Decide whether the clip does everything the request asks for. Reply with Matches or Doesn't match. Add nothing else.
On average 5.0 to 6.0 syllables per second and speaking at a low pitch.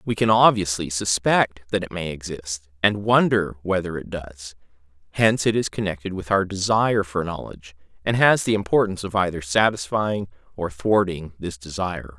Matches